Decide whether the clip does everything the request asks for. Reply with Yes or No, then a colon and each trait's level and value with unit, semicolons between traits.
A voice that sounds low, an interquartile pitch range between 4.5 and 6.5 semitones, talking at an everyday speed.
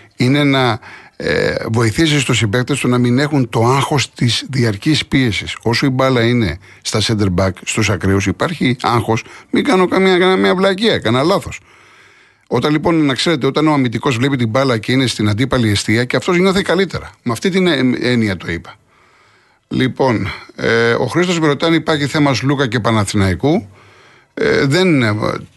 Yes: low, 130 Hz; average, 5.1 semitones; average, 160 wpm